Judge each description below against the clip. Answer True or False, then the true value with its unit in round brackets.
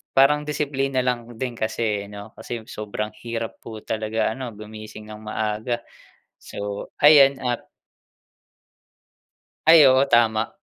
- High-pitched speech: False (115 Hz)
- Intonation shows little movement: False (3.5 semitones)